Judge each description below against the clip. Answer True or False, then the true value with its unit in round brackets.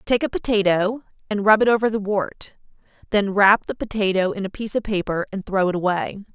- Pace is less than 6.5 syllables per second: True (5.8 syllables/s)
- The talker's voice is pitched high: True (200 Hz)